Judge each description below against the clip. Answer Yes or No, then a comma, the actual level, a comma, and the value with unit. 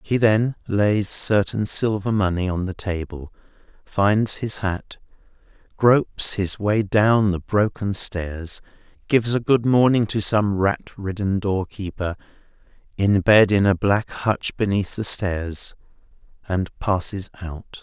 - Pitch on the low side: Yes, low, 100 Hz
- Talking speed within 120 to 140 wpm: Yes, slow, 135 wpm